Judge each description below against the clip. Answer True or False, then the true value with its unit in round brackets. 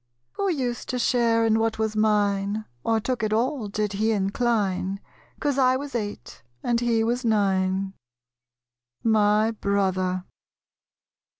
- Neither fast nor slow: False (130 wpm)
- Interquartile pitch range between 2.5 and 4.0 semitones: True (2.9 semitones)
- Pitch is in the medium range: False (220 Hz)